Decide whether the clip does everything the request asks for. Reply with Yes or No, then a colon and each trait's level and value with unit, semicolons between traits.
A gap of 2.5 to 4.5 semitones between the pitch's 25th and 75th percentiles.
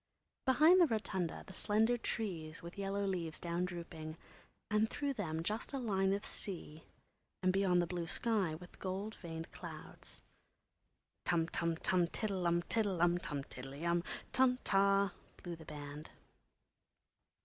Yes: average, 3.8 semitones